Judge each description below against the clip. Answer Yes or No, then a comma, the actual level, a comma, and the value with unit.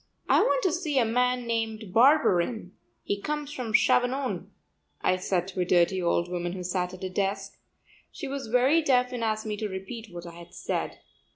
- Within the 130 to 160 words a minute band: No, average, 195 wpm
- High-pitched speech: Yes, high, 220 Hz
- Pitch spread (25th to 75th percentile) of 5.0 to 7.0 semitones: Yes, average, 5.3 semitones